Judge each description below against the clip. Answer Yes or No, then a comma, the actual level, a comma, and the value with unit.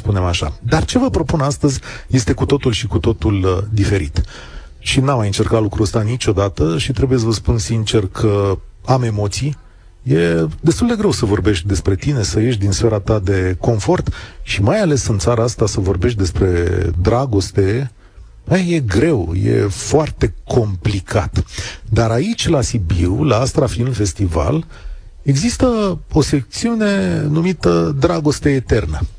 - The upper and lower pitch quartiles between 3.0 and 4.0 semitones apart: No, wide, 5.6 semitones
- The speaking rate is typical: Yes, average, 150 wpm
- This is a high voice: No, low, 110 Hz